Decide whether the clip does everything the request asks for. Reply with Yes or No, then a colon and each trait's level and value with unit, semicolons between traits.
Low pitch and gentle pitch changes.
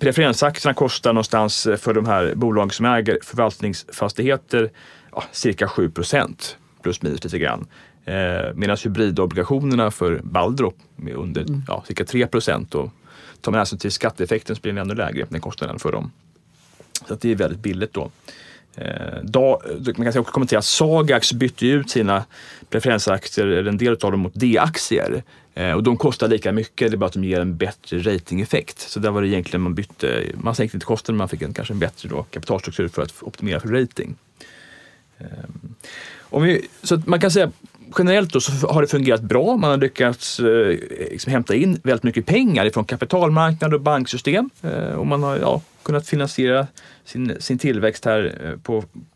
No: low, 120 Hz; average, 4.6 semitones